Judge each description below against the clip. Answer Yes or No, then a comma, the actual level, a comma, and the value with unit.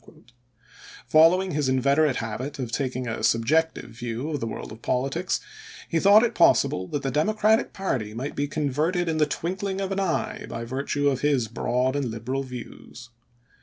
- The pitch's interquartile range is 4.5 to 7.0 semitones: Yes, average, 4.8 semitones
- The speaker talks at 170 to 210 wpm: Yes, average, 175 wpm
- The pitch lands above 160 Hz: No, medium, 140 Hz